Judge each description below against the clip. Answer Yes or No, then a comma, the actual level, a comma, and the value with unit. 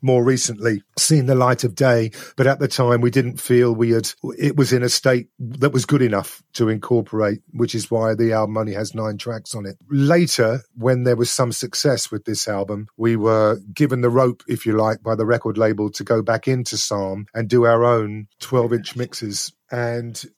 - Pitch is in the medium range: No, low, 120 Hz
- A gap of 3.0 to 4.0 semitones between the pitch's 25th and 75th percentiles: No, narrow, 2.6 semitones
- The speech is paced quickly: Yes, fast, 210 wpm